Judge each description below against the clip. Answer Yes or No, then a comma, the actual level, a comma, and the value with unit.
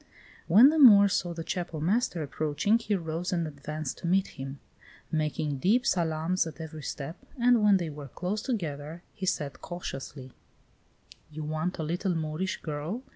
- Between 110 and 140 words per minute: No, average, 165 wpm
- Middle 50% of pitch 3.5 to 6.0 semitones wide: Yes, average, 3.8 semitones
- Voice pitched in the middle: Yes, medium, 165 Hz